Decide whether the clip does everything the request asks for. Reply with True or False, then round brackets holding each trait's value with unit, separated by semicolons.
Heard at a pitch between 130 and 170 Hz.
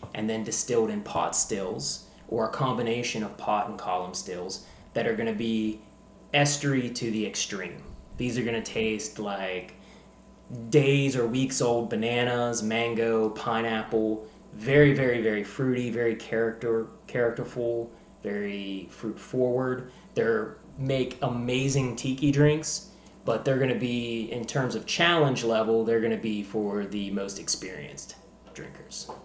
False (115 Hz)